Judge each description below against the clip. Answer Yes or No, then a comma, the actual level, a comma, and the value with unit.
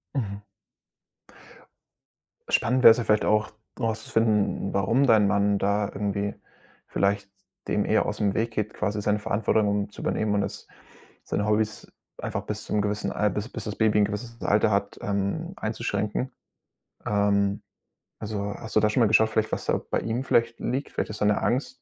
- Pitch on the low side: Yes, low, 105 Hz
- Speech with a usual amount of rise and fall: No, narrow, 1.6 semitones